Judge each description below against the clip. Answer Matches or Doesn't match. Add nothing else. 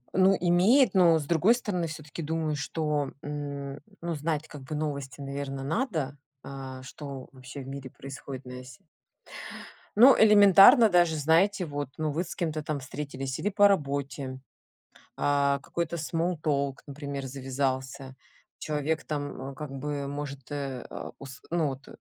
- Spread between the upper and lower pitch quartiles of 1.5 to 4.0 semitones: Matches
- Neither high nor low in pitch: Matches